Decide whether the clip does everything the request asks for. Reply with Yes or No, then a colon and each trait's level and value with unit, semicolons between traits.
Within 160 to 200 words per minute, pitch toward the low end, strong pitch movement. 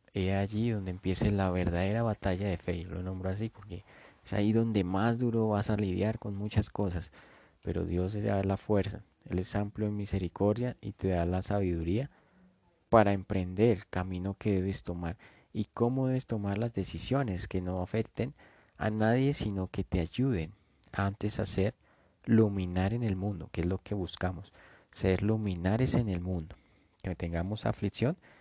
No: average, 175 wpm; low, 100 Hz; average, 2.9 semitones